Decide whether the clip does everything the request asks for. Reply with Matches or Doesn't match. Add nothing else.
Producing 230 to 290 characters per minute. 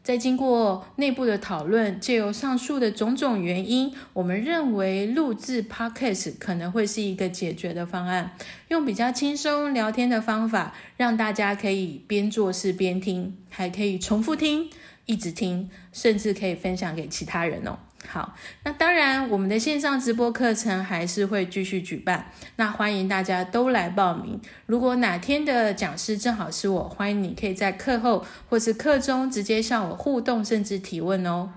Matches